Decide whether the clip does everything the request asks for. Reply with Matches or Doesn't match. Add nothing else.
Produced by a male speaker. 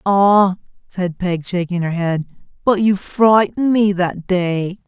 Doesn't match